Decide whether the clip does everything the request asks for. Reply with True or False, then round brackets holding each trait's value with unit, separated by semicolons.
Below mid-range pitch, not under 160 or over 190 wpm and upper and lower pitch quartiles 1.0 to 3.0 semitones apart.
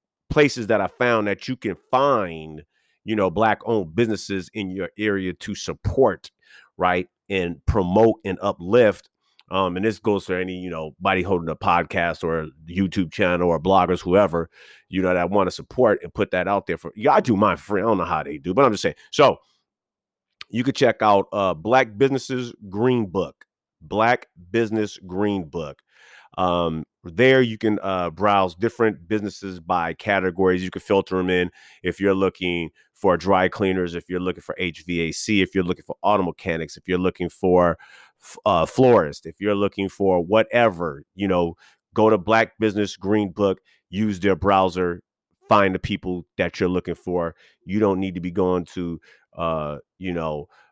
True (95 Hz; 185 wpm; 2.7 semitones)